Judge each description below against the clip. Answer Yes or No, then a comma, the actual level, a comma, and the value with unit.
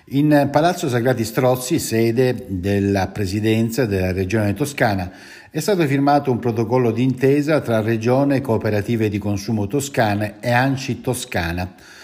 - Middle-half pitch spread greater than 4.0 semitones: Yes, average, 4.5 semitones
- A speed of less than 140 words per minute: Yes, average, 125 wpm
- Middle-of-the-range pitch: No, low, 120 Hz